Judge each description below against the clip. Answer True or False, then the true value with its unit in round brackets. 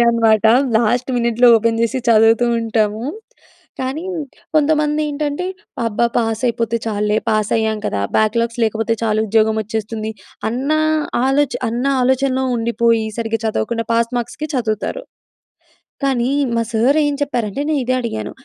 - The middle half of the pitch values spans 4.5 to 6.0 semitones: False (2.9 semitones)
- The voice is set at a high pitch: True (230 Hz)